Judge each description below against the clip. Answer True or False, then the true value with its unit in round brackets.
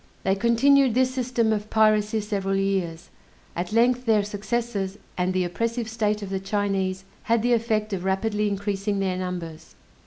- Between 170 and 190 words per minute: False (160 wpm)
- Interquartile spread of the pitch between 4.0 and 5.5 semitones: False (3.0 semitones)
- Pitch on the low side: False (210 Hz)